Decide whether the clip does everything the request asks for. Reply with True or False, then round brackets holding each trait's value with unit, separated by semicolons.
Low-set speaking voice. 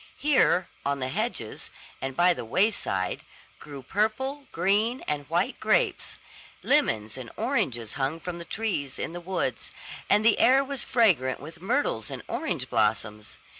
False (170 Hz)